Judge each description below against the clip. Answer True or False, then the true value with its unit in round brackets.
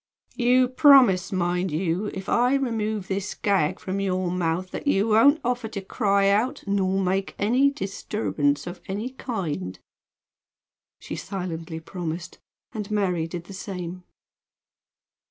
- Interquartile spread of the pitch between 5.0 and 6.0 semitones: False (3.7 semitones)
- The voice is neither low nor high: False (195 Hz)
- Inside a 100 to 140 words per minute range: True (135 wpm)